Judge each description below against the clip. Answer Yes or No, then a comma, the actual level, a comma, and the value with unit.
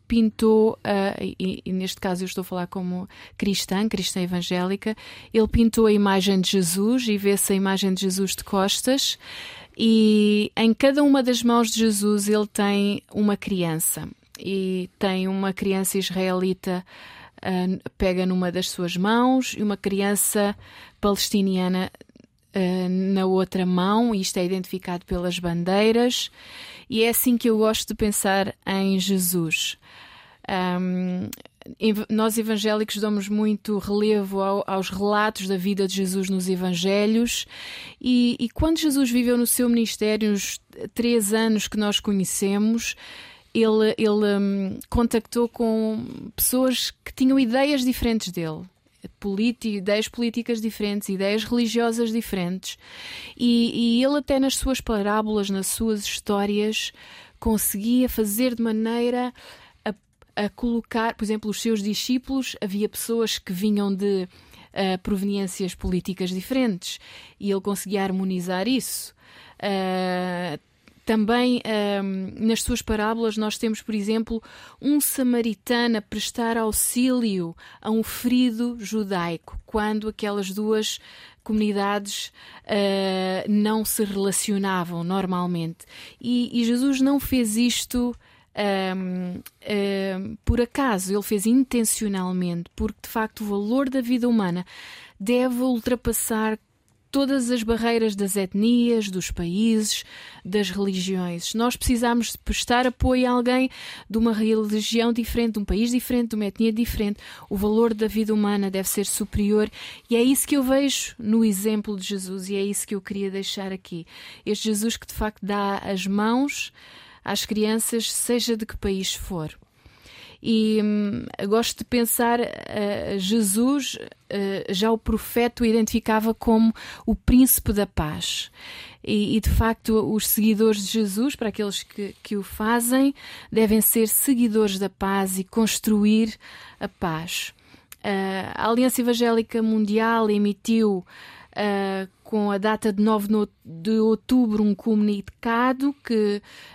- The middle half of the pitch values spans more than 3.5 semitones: No, average, 2.9 semitones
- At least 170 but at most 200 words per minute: No, average, 135 wpm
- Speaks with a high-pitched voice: Yes, high, 215 Hz